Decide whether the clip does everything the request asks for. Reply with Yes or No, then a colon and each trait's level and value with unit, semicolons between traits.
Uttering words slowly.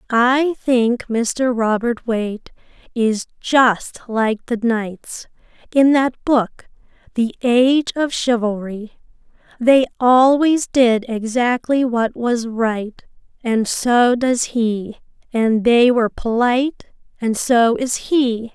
Yes: slow, 115 wpm